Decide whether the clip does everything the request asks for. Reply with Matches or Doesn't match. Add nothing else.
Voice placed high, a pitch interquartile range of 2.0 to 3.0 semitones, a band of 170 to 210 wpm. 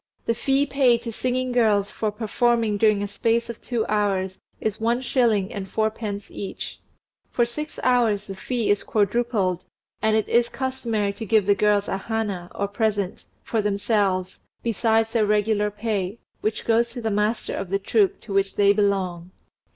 Matches